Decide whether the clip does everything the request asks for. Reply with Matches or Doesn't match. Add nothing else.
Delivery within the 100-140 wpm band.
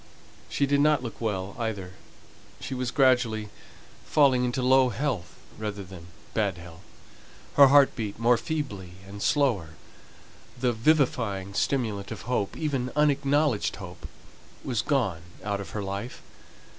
Matches